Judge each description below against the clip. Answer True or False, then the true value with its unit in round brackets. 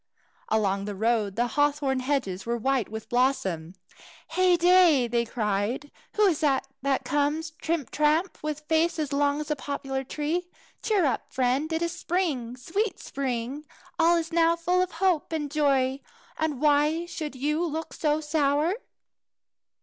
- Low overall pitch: False (290 Hz)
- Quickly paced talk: False (155 wpm)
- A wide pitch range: False (4.3 semitones)